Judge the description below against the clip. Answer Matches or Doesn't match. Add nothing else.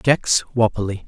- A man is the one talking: Matches